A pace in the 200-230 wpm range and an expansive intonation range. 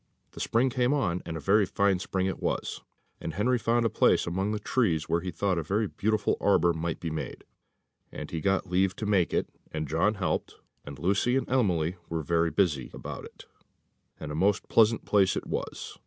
No: fast, 205 wpm; average, 4.1 semitones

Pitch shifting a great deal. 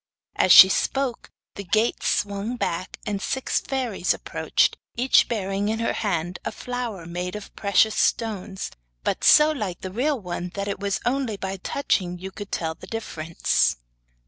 No: average, 3.9 semitones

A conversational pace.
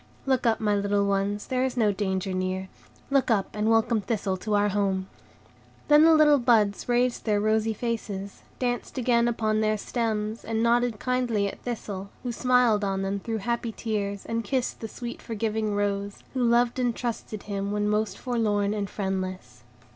Yes: average, 175 wpm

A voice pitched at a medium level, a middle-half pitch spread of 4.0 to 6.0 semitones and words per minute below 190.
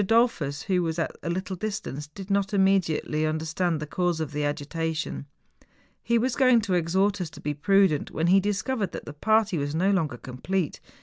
No: medium, 180 Hz; average, 4.3 semitones; average, 195 wpm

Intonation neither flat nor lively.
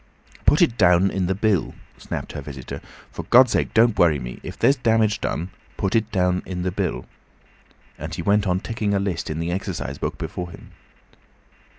Yes: average, 3.9 semitones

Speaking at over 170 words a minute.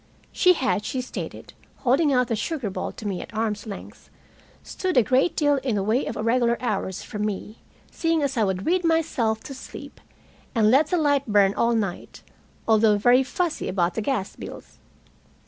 Yes: average, 185 wpm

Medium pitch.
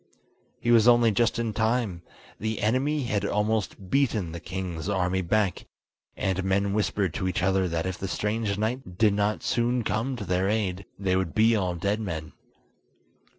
No: low, 100 Hz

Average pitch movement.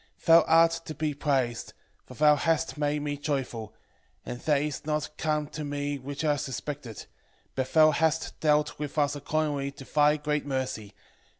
No: narrow, 1.7 semitones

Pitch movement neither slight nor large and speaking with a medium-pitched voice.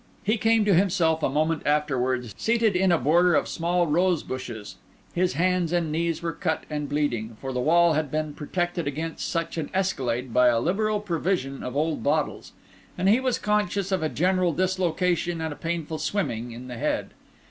Yes: average, 4.0 semitones; medium, 165 Hz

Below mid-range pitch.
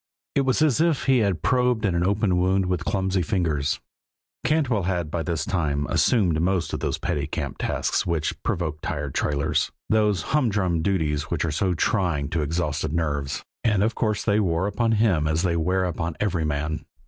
Yes: very low, 90 Hz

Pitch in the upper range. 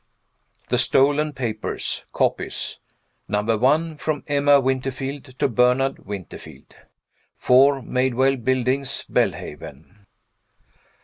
No: low, 130 Hz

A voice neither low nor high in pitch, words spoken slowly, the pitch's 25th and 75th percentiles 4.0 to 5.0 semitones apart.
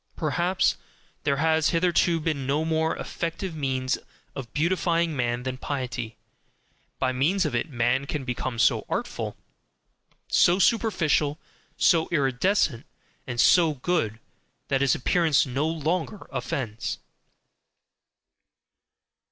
Yes: medium, 150 Hz; slow, 110 wpm; average, 4.4 semitones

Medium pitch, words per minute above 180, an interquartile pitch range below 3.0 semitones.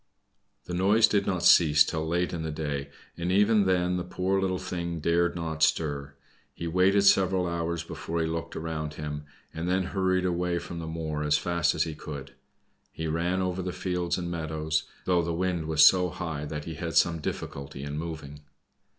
No: very low, 85 Hz; average, 190 wpm; narrow, 2.5 semitones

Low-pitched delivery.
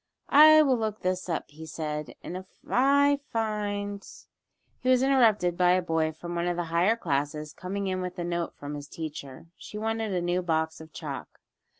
No: medium, 180 Hz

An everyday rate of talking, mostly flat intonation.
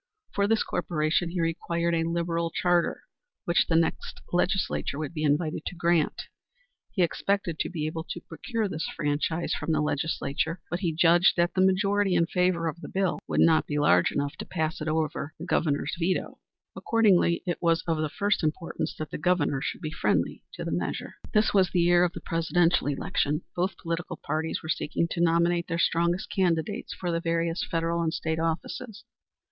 Yes: average, 190 wpm; narrow, 1.9 semitones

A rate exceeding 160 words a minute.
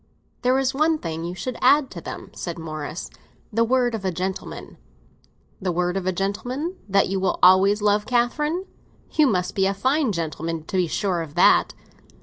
Yes: average, 190 wpm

